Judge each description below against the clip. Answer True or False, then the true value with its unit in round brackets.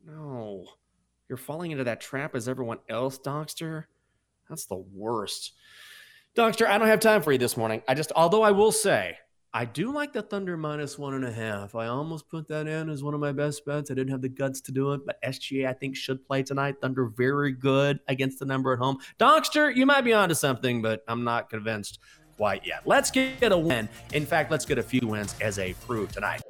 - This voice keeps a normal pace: False (225 wpm)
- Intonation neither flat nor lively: True (4.3 semitones)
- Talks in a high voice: False (140 Hz)